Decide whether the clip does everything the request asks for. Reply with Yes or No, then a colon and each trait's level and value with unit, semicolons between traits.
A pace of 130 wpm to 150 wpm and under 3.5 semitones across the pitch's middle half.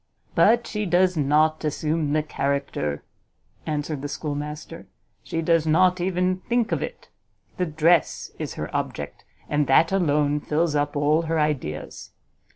Yes: average, 145 wpm; average, 2.7 semitones